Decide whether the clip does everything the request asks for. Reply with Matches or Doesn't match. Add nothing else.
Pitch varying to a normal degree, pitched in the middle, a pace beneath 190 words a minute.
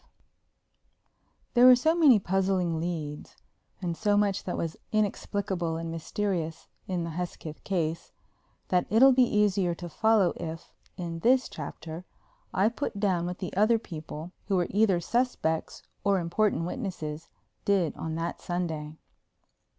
Matches